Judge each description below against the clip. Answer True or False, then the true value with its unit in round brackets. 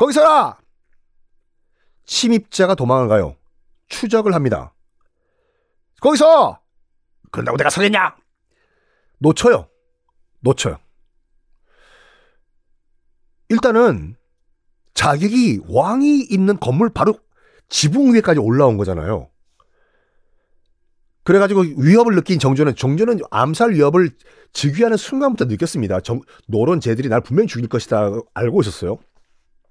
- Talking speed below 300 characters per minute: True (240 characters per minute)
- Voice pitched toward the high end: True (210 Hz)